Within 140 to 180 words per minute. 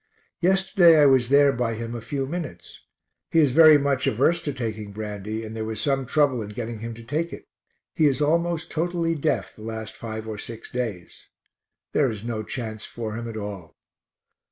No: average, 195 wpm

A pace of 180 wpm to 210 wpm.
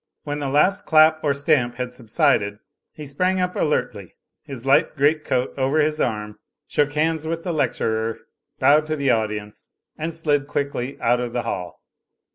No: average, 170 wpm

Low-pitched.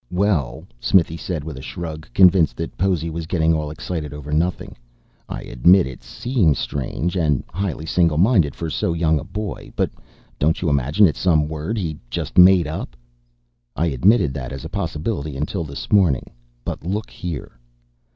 Yes: very low, 80 Hz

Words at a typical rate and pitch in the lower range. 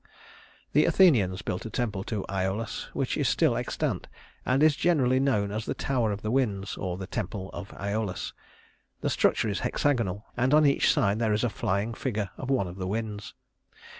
Yes: average, 190 wpm; low, 105 Hz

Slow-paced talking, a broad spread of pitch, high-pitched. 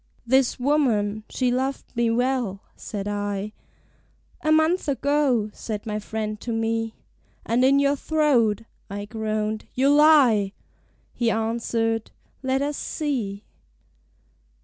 No: slow, 120 wpm; average, 4.3 semitones; high, 230 Hz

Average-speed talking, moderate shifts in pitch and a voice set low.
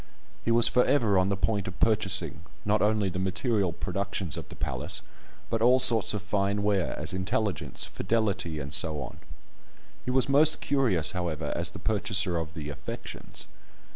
Yes: average, 175 wpm; average, 4.0 semitones; low, 100 Hz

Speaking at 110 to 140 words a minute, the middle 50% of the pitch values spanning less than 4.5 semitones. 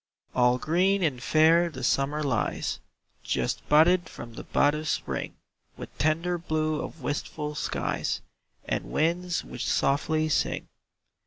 Yes: slow, 135 wpm; average, 2.7 semitones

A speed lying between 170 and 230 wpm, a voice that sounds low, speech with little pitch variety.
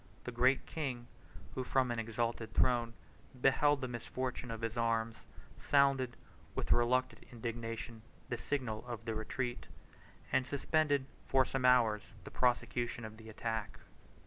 No: average, 140 wpm; low, 120 Hz; narrow, 2.1 semitones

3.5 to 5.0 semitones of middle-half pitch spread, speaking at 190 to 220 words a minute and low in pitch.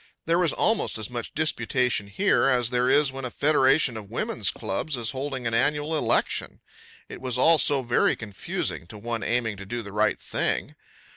Yes: average, 4.2 semitones; average, 195 wpm; low, 125 Hz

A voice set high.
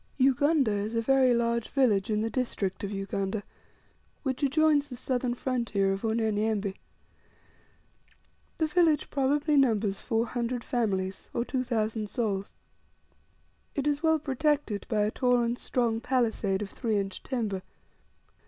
Yes: high, 235 Hz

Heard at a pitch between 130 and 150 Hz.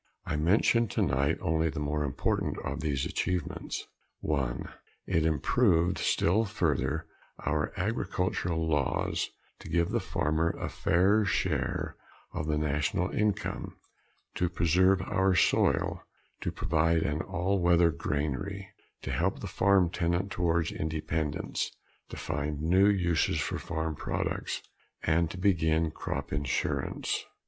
No: very low, 80 Hz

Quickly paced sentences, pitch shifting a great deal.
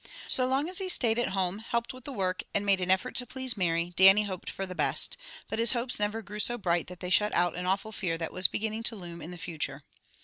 No: fast, 265 wpm; average, 4.4 semitones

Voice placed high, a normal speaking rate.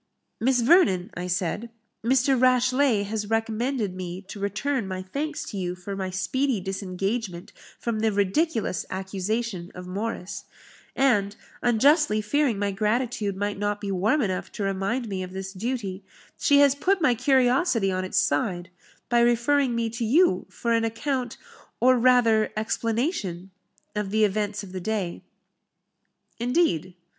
Yes: high, 215 Hz; average, 150 wpm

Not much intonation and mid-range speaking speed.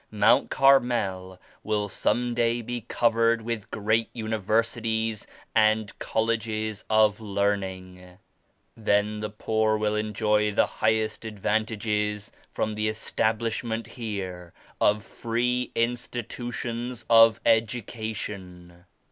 No: narrow, 1.7 semitones; slow, 95 wpm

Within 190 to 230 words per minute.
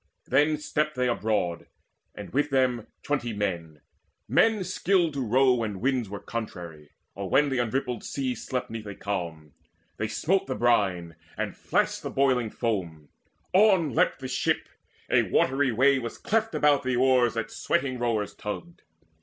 No: average, 160 wpm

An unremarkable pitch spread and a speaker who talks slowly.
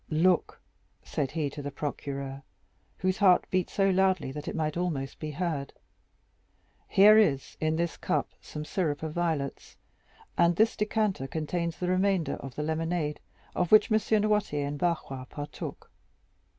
No: average, 4.2 semitones; average, 150 wpm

